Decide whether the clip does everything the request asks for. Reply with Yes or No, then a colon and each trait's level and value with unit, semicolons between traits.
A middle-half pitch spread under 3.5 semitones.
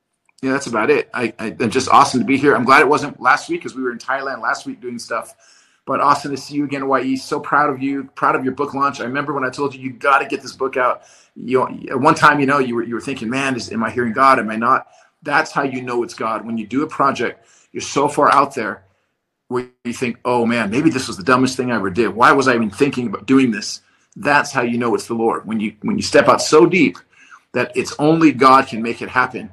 Yes: average, 2.7 semitones